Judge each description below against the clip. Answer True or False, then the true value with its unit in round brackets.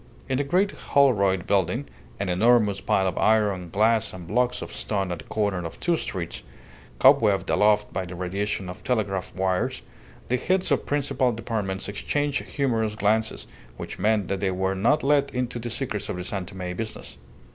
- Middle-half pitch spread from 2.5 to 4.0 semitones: False (4.7 semitones)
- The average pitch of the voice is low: True (105 Hz)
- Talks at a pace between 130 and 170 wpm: False (180 wpm)